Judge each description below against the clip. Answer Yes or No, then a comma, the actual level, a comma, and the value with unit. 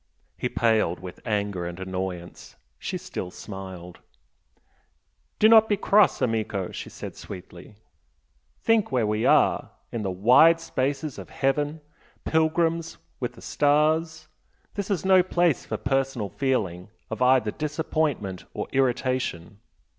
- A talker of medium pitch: No, low, 130 Hz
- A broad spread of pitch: Yes, wide, 8.4 semitones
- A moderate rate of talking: No, slow, 130 wpm